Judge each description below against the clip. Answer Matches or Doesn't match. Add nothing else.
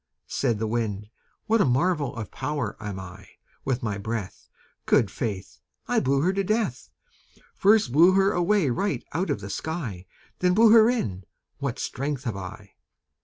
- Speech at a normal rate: Matches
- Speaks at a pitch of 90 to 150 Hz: Matches